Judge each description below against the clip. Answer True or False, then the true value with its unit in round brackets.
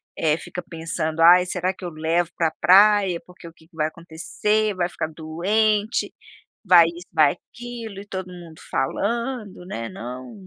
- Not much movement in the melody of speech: False (3.9 semitones)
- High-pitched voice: False (175 Hz)